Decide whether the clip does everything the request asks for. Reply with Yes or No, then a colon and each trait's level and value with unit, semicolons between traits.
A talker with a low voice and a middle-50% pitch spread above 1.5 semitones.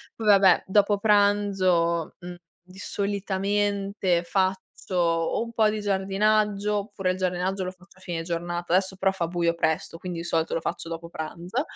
No: high, 190 Hz; average, 2.7 semitones